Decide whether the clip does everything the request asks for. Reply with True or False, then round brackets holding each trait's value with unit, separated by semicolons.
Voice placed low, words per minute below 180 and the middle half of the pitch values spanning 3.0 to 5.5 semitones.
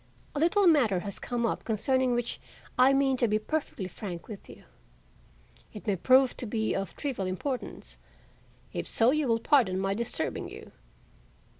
False (235 Hz; 165 wpm; 4.8 semitones)